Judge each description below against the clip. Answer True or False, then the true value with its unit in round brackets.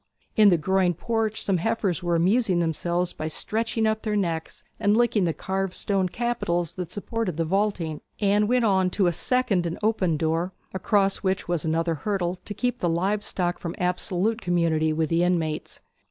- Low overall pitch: False (185 Hz)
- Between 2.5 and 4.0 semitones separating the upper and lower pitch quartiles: True (3.7 semitones)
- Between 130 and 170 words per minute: False (185 wpm)